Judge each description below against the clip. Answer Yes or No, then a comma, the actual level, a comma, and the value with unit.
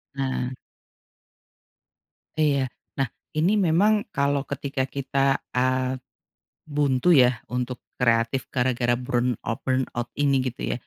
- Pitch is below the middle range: Yes, low, 130 Hz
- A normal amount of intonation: No, narrow, 2.1 semitones